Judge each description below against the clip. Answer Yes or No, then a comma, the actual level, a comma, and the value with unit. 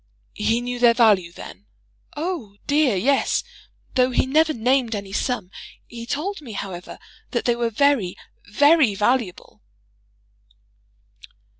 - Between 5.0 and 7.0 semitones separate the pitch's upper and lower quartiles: Yes, average, 5.3 semitones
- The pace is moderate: No, slow, 125 wpm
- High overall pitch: Yes, high, 240 Hz